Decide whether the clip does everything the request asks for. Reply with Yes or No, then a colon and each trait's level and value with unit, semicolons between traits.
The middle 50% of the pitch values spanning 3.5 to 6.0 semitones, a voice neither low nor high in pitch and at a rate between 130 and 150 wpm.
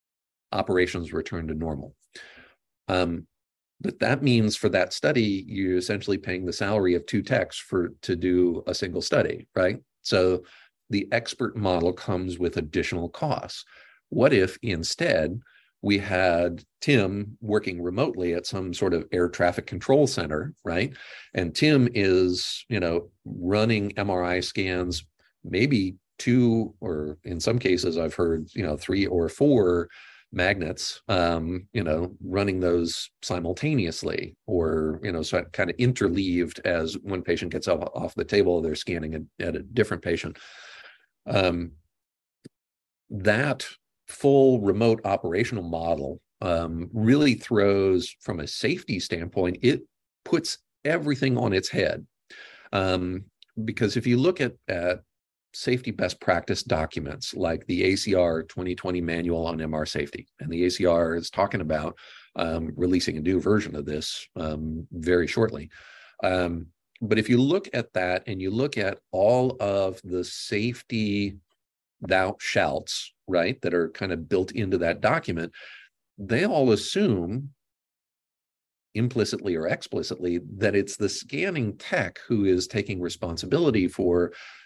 No: average, 4.0 semitones; very low, 90 Hz; average, 140 wpm